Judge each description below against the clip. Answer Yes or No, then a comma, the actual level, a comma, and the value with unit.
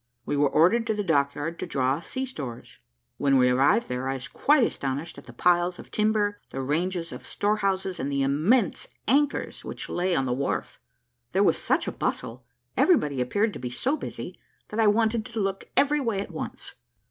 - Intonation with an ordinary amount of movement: No, wide, 7.8 semitones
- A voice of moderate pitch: Yes, medium, 175 Hz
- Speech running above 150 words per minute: Yes, average, 195 wpm